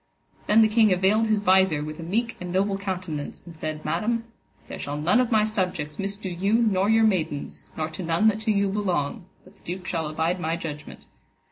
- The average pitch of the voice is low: No, medium, 185 Hz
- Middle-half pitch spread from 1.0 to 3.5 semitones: No, average, 4.7 semitones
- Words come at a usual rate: No, fast, 210 wpm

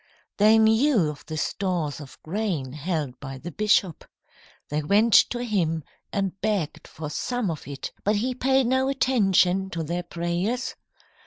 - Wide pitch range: Yes, wide, 5.8 semitones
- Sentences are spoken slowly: No, average, 155 wpm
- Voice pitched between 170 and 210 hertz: Yes, high, 190 Hz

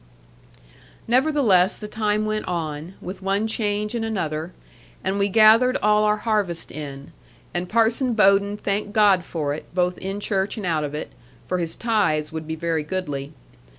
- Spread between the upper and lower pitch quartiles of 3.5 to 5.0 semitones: Yes, average, 4.4 semitones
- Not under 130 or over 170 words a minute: Yes, average, 165 wpm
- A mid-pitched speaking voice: No, high, 195 Hz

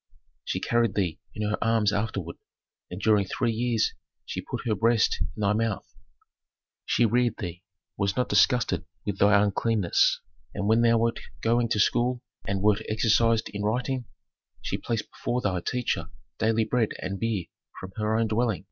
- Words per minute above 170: No, average, 165 wpm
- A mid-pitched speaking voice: No, low, 110 Hz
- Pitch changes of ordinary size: No, narrow, 2.3 semitones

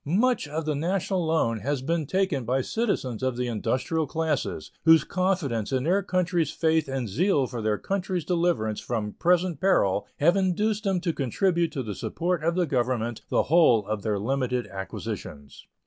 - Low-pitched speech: No, medium, 155 Hz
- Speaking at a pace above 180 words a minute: No, average, 175 wpm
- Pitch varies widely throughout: Yes, wide, 6.6 semitones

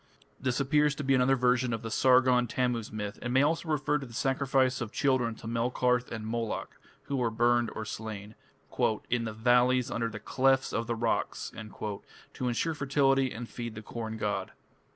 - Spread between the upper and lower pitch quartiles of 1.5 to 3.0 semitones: Yes, average, 2.7 semitones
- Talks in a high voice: No, low, 120 Hz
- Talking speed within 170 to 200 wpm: Yes, average, 185 wpm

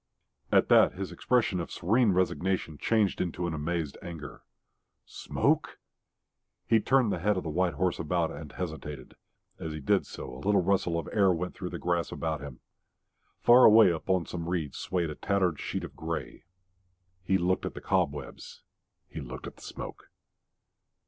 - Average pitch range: Yes, average, 3.3 semitones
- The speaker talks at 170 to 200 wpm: Yes, average, 175 wpm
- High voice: No, very low, 90 Hz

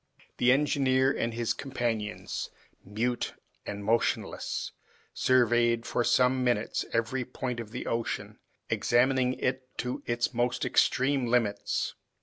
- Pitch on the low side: Yes, low, 120 Hz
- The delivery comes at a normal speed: No, slow, 120 wpm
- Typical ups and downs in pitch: No, narrow, 1.7 semitones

